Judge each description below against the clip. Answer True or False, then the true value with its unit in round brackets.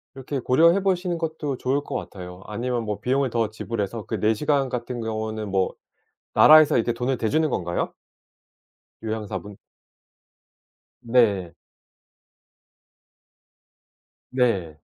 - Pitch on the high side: False (120 Hz)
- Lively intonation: False (4.5 semitones)